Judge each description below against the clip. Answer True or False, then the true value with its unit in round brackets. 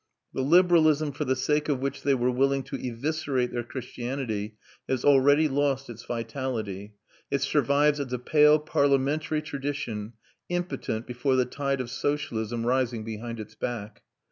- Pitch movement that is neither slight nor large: True (3.2 semitones)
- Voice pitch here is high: False (135 Hz)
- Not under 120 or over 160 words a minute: True (150 wpm)